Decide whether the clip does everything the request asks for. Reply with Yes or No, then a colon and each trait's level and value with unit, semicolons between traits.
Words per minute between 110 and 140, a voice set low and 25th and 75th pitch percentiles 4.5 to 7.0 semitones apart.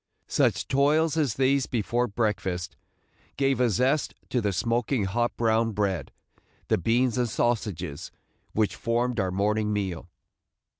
No: slow, 135 wpm; low, 115 Hz; average, 3.6 semitones